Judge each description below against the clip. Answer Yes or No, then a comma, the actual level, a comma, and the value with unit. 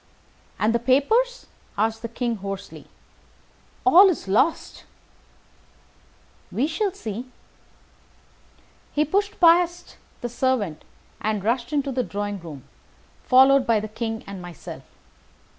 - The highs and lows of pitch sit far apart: Yes, wide, 6.5 semitones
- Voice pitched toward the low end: No, high, 240 Hz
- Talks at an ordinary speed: No, slow, 115 wpm